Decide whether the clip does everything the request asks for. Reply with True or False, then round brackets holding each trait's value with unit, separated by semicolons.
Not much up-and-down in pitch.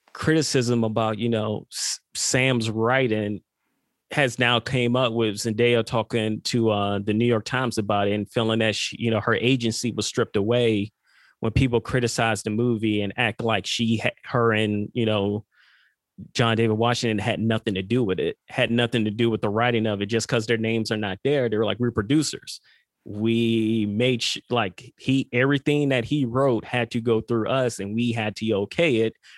True (2.0 semitones)